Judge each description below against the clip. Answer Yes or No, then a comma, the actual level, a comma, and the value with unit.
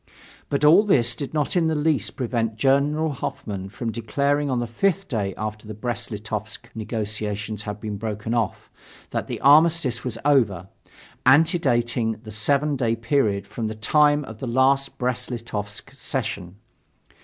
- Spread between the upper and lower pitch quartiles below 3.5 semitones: No, average, 4.7 semitones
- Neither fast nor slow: Yes, average, 155 wpm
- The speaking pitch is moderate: No, low, 120 Hz